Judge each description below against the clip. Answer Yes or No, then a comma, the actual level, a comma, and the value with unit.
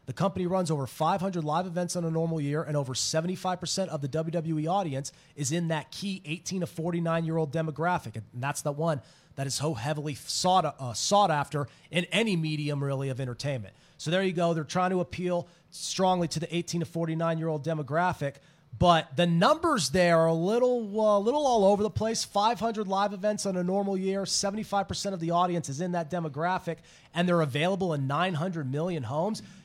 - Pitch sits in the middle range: Yes, medium, 170 Hz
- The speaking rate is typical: No, fast, 225 wpm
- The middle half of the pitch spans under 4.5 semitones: Yes, average, 3.3 semitones